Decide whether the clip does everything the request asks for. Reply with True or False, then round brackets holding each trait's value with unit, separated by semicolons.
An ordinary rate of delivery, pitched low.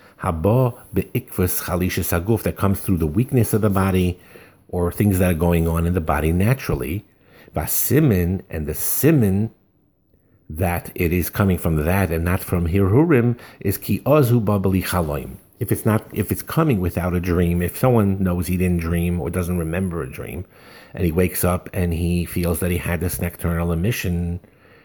True (160 wpm; 90 Hz)